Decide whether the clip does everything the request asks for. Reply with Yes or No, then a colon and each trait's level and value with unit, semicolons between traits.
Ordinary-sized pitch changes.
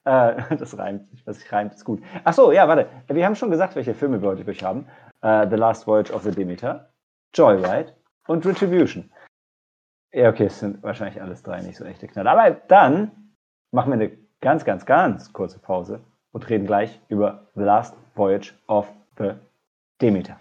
No: wide, 6.7 semitones